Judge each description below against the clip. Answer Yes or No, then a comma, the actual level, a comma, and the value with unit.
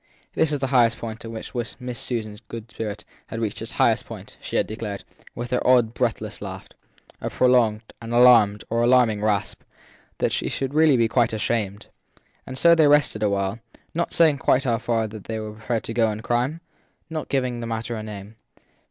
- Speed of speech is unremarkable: Yes, average, 190 wpm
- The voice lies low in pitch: Yes, low, 115 Hz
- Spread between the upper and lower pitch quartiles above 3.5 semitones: No, average, 2.7 semitones